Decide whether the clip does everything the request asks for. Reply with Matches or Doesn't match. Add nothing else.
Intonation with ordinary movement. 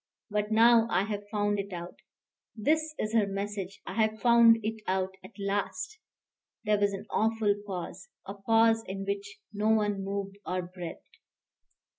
Doesn't match